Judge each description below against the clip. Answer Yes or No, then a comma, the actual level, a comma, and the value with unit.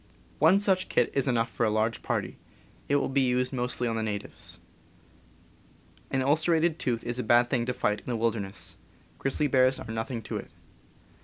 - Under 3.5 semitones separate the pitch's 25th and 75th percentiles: Yes, average, 3.0 semitones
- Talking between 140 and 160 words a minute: No, average, 200 wpm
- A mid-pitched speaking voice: No, low, 125 Hz